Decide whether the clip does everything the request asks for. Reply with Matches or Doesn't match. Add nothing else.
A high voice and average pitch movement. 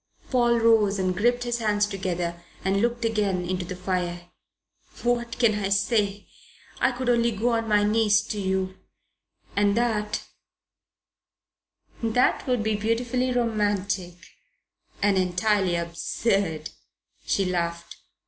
Matches